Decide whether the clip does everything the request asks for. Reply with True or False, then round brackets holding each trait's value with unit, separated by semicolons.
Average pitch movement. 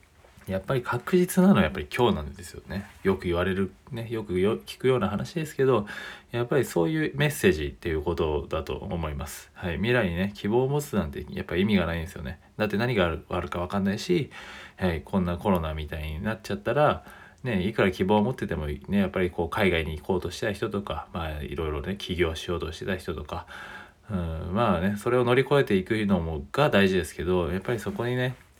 False (5.7 semitones)